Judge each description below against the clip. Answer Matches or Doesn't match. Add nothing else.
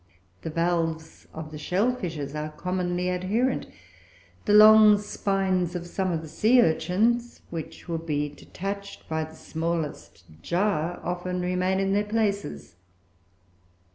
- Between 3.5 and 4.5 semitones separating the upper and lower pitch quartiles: Matches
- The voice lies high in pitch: Doesn't match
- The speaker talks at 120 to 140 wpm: Matches